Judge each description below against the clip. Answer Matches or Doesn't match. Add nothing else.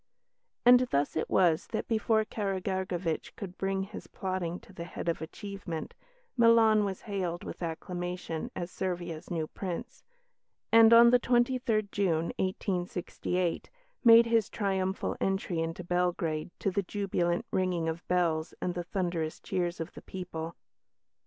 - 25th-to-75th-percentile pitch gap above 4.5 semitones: Doesn't match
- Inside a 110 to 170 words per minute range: Matches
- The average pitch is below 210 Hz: Matches